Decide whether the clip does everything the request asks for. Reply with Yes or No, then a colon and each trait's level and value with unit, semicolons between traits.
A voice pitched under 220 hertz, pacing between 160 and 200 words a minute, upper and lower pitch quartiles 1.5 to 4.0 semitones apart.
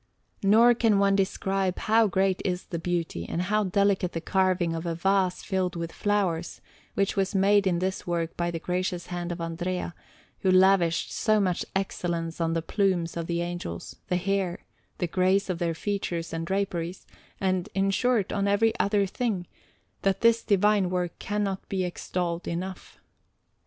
Yes: medium, 185 Hz; average, 170 wpm; narrow, 2.4 semitones